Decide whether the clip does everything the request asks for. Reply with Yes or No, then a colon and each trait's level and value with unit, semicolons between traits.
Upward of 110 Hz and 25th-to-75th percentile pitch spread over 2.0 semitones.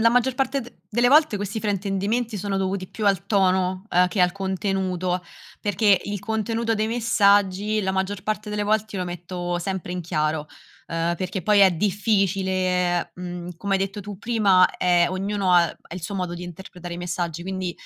Yes: high, 190 Hz; narrow, 2.5 semitones